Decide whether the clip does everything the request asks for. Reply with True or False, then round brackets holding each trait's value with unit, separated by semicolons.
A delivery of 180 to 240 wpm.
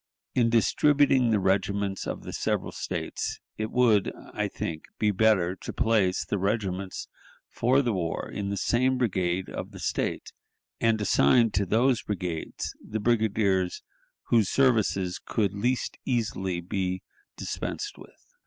False (140 wpm)